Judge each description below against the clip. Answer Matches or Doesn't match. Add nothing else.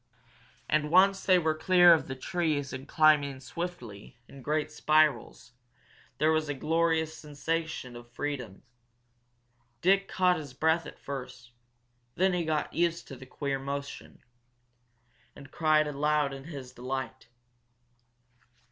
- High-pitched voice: Doesn't match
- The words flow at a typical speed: Doesn't match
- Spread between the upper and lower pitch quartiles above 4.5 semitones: Doesn't match